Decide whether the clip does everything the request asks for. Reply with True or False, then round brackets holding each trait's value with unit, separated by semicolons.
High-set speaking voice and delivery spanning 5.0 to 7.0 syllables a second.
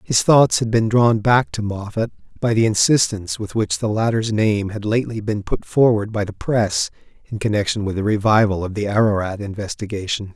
False (105 Hz; 5.3 syllables/s)